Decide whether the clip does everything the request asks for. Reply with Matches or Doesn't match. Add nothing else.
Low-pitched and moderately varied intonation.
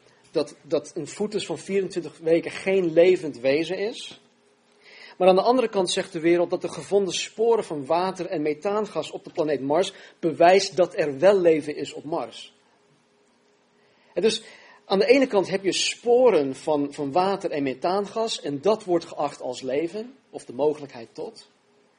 Doesn't match